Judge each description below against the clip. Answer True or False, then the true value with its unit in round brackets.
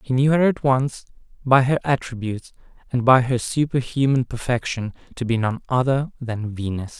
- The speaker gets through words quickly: False (165 wpm)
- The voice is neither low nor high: False (125 Hz)